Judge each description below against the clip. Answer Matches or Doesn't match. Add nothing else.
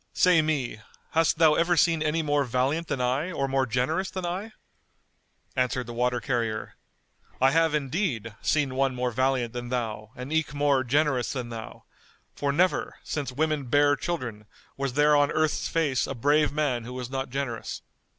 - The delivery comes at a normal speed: Matches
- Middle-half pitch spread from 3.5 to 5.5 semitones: Matches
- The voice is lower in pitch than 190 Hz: Matches